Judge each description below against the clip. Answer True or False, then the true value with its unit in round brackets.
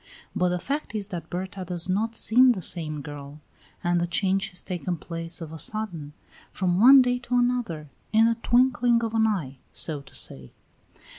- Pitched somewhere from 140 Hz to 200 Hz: True (185 Hz)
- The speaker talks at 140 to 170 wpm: False (190 wpm)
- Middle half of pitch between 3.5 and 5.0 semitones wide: False (5.5 semitones)